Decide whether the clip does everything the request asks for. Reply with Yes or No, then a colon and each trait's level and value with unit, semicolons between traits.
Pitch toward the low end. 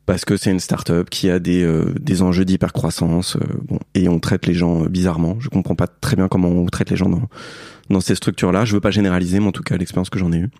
Yes: very low, 90 Hz